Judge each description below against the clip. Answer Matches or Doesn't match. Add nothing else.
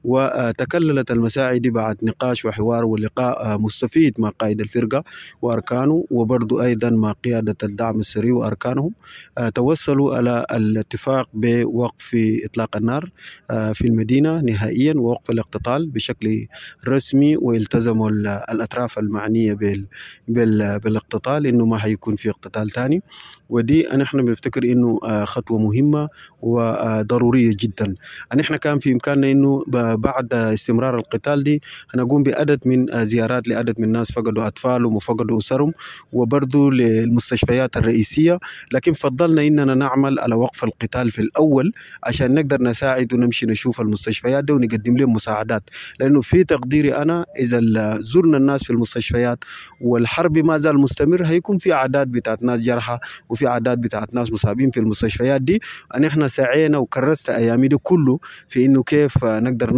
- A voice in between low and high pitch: Doesn't match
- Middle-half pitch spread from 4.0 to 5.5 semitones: Doesn't match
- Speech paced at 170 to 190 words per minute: Doesn't match